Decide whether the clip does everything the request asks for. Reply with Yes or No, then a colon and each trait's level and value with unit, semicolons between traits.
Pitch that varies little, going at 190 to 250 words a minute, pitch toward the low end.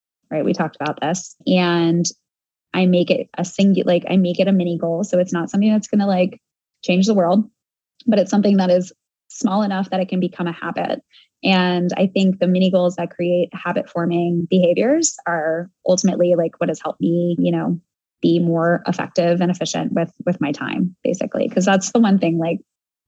No: narrow, 2.0 semitones; fast, 205 wpm; medium, 180 Hz